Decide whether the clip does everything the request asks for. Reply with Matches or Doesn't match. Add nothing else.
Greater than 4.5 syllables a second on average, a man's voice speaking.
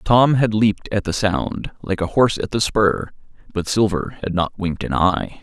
Matches